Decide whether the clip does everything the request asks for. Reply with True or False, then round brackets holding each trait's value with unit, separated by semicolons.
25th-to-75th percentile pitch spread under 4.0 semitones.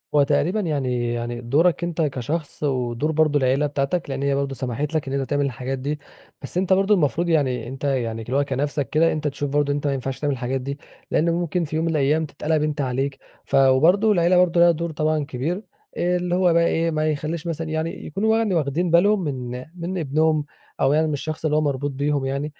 True (3.5 semitones)